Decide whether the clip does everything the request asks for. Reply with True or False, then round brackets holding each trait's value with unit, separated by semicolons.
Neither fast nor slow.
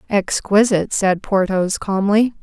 False (100 wpm)